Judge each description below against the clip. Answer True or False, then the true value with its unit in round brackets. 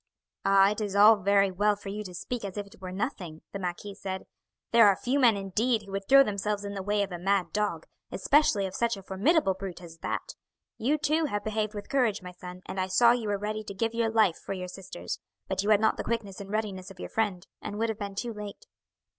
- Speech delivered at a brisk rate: True (250 wpm)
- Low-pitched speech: False (205 Hz)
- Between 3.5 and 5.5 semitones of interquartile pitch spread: False (2.4 semitones)